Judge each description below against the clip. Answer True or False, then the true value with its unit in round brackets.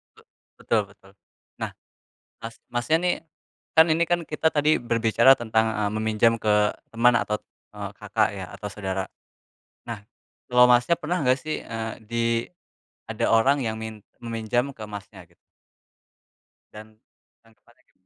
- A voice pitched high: False (115 Hz)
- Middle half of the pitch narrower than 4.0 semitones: True (2.5 semitones)